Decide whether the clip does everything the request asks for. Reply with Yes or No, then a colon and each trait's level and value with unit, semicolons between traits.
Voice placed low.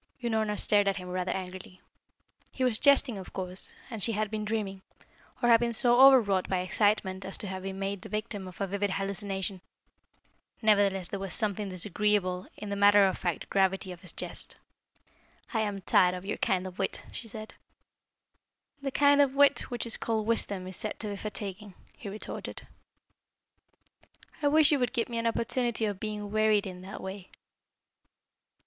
No: high, 205 Hz